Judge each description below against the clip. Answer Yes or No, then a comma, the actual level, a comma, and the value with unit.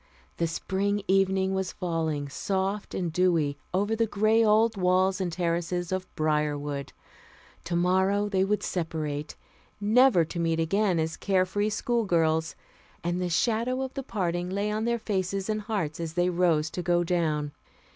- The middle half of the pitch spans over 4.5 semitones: No, average, 3.7 semitones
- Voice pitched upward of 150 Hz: Yes, medium, 185 Hz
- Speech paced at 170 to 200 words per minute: No, average, 155 wpm